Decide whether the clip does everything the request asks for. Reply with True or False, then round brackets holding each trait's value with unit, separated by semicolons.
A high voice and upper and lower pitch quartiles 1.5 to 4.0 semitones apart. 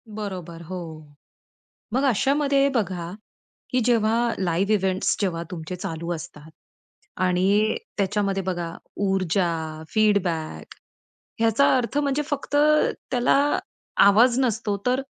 False (200 Hz; 5.2 semitones)